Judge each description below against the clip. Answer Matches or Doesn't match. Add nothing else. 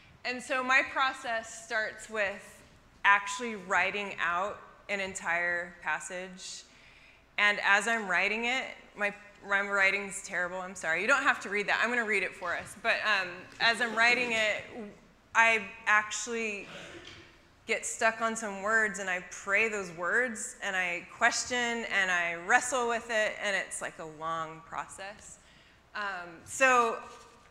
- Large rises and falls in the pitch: Doesn't match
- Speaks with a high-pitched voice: Matches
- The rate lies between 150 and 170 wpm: Matches